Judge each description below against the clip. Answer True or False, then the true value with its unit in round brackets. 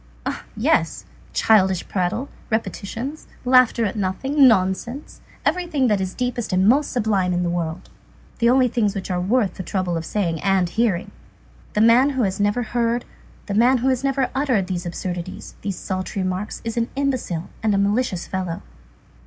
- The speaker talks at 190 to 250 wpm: False (170 wpm)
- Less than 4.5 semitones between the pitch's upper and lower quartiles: False (5.0 semitones)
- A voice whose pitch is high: True (210 Hz)